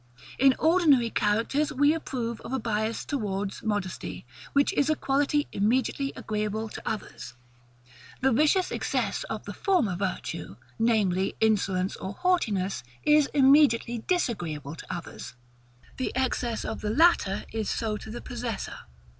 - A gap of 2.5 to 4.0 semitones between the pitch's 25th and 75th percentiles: No, average, 5.3 semitones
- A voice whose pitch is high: Yes, high, 230 Hz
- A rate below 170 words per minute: Yes, average, 140 wpm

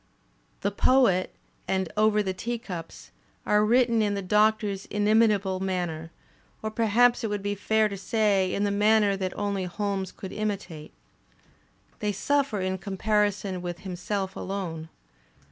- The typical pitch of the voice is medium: No, high, 205 Hz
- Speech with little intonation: Yes, narrow, 2.3 semitones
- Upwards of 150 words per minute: No, average, 140 wpm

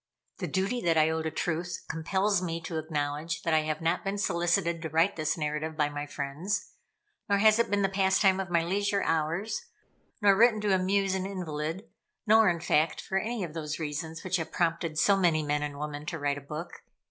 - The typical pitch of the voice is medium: Yes, medium, 170 Hz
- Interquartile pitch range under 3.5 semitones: No, average, 3.8 semitones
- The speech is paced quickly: Yes, fast, 210 wpm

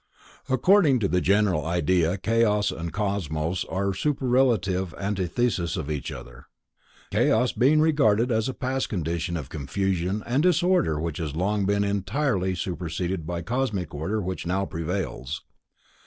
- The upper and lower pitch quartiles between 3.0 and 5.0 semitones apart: No, wide, 5.4 semitones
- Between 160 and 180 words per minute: No, average, 140 wpm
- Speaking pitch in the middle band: No, very low, 95 Hz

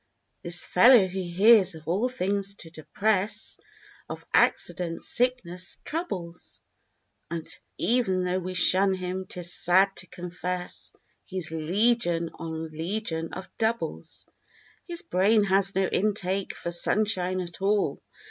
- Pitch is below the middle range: No, medium, 185 Hz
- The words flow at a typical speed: No, slow, 125 wpm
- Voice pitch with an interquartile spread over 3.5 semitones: No, average, 3.0 semitones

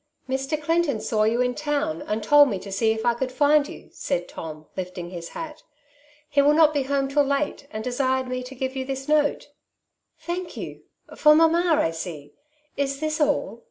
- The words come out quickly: Yes, fast, 210 wpm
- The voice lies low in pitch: No, very high, 270 Hz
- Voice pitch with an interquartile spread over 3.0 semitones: Yes, average, 5.1 semitones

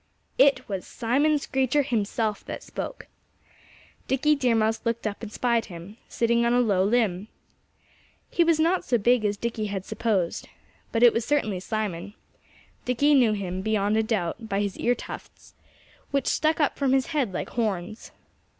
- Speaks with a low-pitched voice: No, high, 230 Hz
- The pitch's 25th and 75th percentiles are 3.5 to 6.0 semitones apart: Yes, average, 4.0 semitones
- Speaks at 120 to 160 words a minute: No, average, 170 wpm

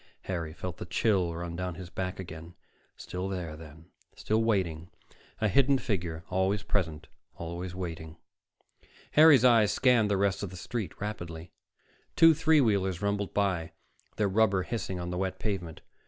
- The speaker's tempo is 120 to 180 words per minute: Yes, average, 155 wpm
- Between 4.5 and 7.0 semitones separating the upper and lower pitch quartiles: No, average, 3.6 semitones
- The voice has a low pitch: Yes, very low, 95 Hz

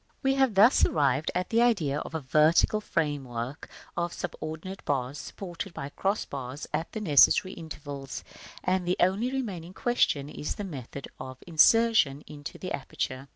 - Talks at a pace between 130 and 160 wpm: No, average, 170 wpm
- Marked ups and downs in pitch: Yes, wide, 5.7 semitones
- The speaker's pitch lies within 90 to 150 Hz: No, medium, 160 Hz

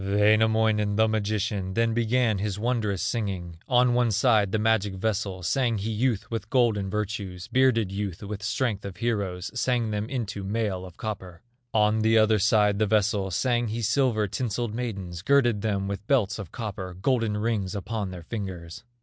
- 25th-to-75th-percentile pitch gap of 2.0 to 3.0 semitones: Yes, average, 2.7 semitones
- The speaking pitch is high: No, low, 105 Hz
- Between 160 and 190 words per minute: Yes, average, 170 wpm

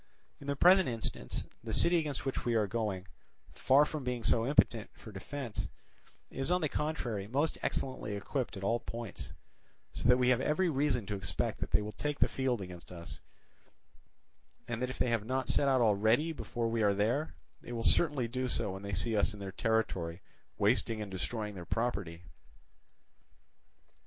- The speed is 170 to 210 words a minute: Yes, average, 185 wpm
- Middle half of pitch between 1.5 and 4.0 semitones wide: No, average, 4.5 semitones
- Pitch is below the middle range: Yes, low, 115 Hz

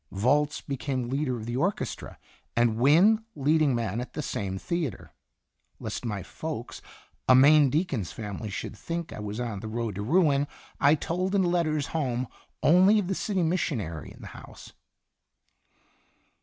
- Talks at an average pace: Yes, average, 155 wpm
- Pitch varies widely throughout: Yes, wide, 6.4 semitones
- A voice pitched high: No, medium, 140 Hz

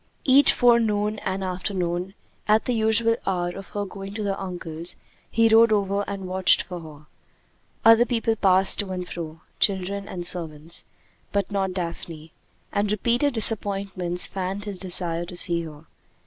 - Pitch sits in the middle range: No, high, 195 Hz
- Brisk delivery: No, average, 155 wpm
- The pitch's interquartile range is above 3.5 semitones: No, average, 3.1 semitones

